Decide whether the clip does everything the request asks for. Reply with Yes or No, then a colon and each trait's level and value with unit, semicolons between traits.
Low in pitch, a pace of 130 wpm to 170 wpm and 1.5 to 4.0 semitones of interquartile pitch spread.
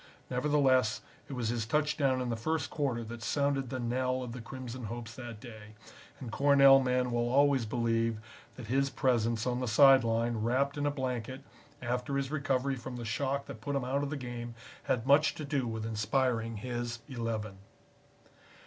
No: low, 125 Hz; average, 185 wpm; average, 2.9 semitones